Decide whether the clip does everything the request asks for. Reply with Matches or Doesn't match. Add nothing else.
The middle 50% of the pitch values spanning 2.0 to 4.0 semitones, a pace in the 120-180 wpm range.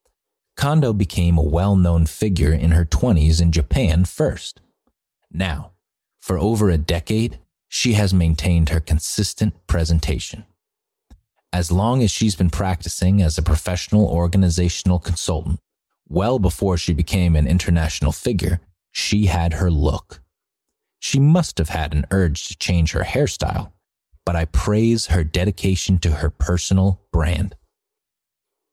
Matches